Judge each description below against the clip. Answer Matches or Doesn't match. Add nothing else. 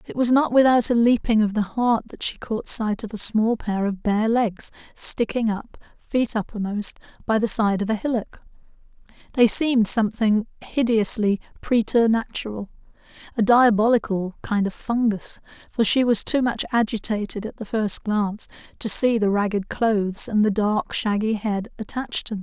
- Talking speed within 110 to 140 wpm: Doesn't match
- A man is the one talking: Doesn't match